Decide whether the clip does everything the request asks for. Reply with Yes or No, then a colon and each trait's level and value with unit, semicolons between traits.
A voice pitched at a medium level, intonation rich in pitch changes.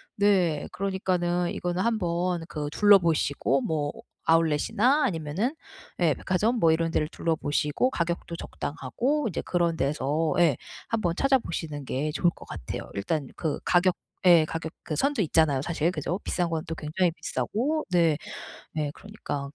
No: medium, 170 Hz; average, 3.7 semitones